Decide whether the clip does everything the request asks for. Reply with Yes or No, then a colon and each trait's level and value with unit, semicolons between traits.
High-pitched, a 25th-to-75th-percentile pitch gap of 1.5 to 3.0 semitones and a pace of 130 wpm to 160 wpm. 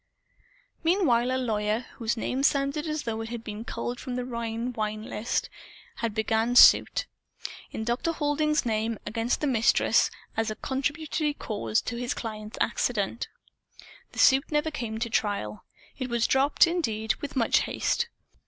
No: high, 235 Hz; average, 4.0 semitones; average, 155 wpm